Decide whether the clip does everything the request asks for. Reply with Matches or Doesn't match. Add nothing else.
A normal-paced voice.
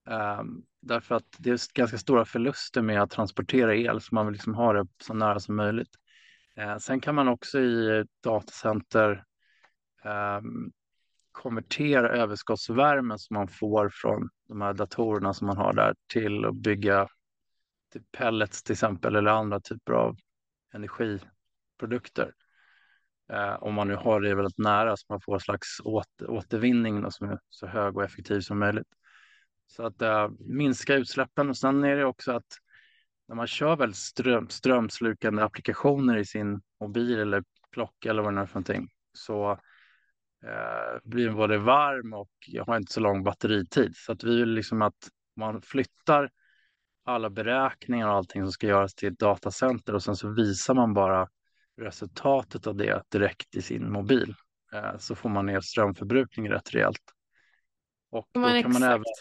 Matches